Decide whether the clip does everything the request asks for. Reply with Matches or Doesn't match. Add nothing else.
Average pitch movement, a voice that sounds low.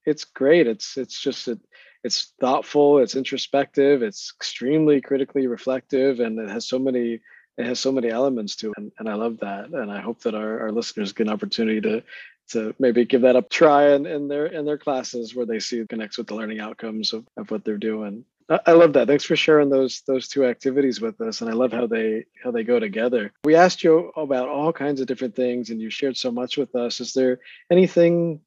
Matches